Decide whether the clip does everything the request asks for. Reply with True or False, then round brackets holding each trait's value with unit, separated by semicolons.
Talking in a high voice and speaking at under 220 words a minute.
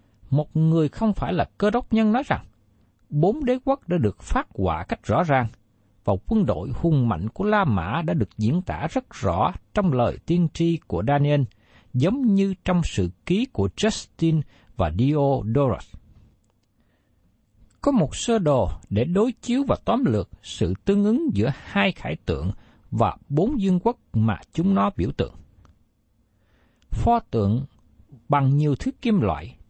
False (130 Hz; 165 wpm)